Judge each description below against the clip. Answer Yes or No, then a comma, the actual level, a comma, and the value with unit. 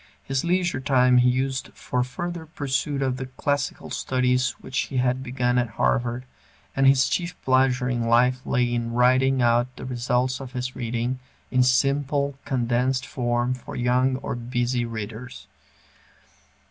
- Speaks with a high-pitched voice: No, low, 125 Hz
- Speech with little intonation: Yes, narrow, 1.4 semitones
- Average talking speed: Yes, average, 150 wpm